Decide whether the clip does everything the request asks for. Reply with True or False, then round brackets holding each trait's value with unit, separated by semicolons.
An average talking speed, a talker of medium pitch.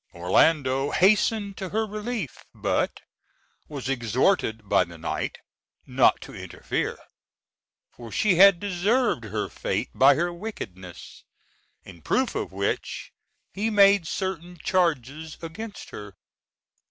False (115 wpm; 165 Hz)